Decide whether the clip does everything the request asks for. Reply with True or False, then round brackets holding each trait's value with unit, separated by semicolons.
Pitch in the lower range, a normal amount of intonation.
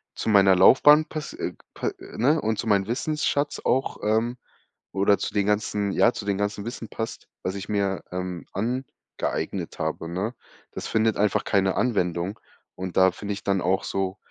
True (100 Hz; 3.1 semitones)